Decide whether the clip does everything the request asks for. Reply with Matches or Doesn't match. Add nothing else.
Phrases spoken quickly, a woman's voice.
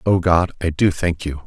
Doesn't match